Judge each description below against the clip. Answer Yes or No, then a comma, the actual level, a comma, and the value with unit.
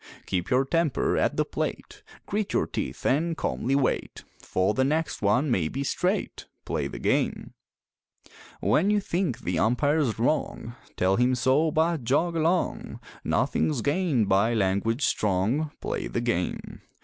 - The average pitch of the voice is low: Yes, low, 130 Hz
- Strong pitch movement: Yes, wide, 6.2 semitones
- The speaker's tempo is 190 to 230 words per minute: No, average, 150 wpm